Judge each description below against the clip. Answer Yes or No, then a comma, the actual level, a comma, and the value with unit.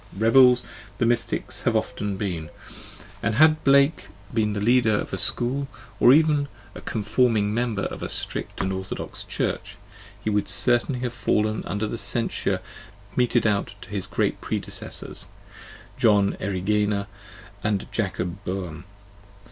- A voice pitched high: No, low, 105 Hz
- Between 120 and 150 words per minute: Yes, average, 140 wpm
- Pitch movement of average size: Yes, average, 3.4 semitones